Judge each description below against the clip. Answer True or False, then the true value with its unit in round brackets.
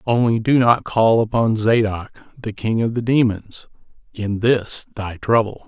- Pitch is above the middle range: False (110 Hz)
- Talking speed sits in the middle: True (160 wpm)